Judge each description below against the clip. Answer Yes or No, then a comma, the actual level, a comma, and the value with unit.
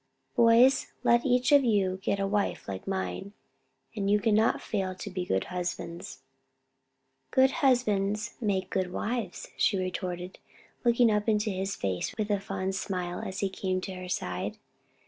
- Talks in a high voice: Yes, high, 195 Hz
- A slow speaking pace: No, average, 165 wpm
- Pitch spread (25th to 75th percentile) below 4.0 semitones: Yes, average, 3.1 semitones